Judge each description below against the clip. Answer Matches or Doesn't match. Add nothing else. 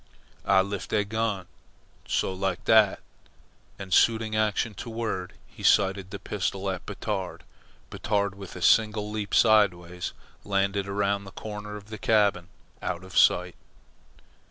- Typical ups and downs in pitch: Doesn't match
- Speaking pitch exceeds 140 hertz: Doesn't match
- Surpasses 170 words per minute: Doesn't match